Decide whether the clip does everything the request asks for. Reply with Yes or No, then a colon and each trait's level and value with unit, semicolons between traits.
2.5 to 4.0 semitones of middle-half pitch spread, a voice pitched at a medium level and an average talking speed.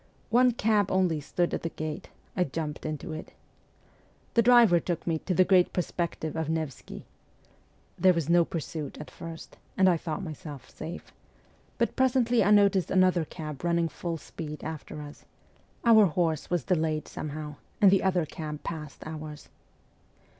Yes: average, 3.2 semitones; medium, 165 Hz; average, 160 wpm